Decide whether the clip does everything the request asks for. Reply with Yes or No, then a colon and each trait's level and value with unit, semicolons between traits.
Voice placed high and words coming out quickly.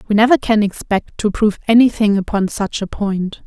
Yes: high, 210 Hz; fast, 210 wpm